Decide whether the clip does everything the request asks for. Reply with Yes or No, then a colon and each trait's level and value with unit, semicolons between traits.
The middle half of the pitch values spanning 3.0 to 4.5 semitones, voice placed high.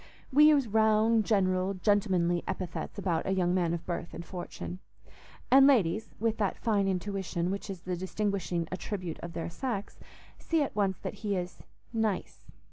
Yes: average, 3.3 semitones; high, 195 Hz